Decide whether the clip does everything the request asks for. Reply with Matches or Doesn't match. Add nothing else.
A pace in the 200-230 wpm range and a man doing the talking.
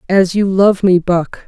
Doesn't match